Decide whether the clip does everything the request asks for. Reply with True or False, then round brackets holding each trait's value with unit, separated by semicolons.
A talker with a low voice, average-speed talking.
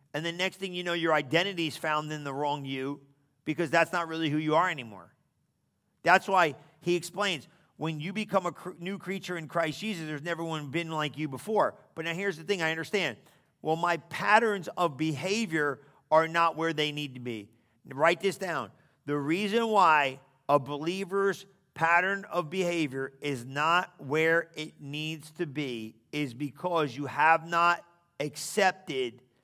False (160 Hz; 175 wpm)